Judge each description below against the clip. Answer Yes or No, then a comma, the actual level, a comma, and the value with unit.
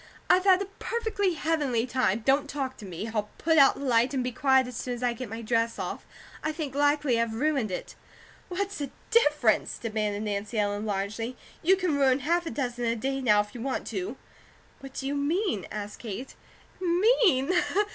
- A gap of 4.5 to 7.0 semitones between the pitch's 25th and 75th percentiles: Yes, average, 5.2 semitones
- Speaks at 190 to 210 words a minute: Yes, average, 195 wpm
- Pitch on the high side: Yes, very high, 260 Hz